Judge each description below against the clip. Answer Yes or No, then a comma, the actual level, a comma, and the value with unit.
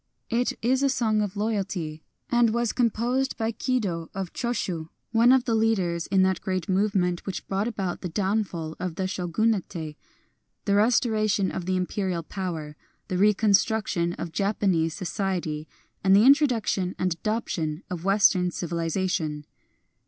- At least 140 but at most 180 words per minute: Yes, average, 150 wpm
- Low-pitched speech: No, high, 195 Hz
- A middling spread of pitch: Yes, average, 4.0 semitones